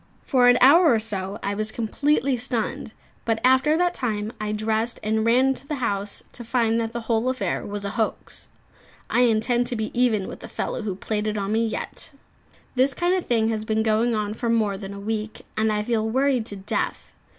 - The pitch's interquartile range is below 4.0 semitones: Yes, narrow, 2.6 semitones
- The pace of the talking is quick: Yes, fast, 215 wpm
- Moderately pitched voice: No, high, 225 Hz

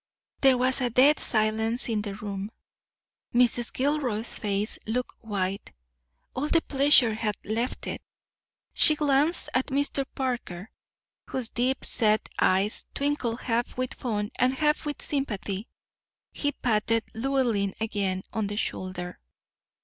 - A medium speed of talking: No, slow, 125 wpm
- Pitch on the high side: Yes, high, 230 Hz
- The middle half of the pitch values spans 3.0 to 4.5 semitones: Yes, average, 4.0 semitones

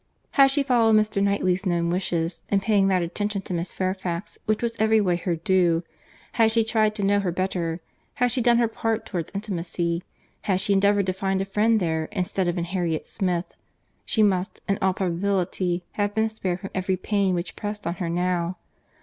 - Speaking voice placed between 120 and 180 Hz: No, high, 190 Hz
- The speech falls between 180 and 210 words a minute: Yes, average, 200 wpm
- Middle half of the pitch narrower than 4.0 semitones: Yes, average, 3.0 semitones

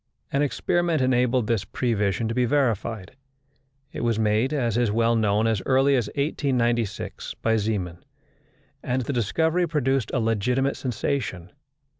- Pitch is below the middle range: Yes, low, 120 Hz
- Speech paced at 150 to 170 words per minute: No, average, 140 wpm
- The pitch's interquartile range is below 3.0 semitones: No, average, 3.5 semitones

